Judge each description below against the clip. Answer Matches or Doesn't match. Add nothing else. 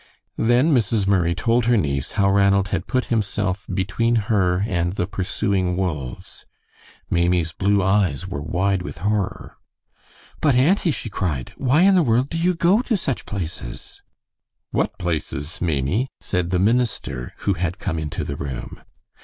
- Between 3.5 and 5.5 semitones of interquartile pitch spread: Matches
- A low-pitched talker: Matches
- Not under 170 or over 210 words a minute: Doesn't match